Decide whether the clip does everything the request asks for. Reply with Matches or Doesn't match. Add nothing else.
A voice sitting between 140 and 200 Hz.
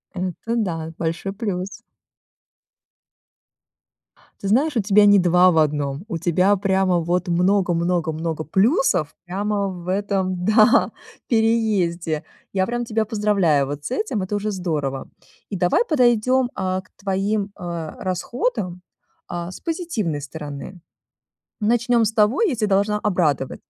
Matches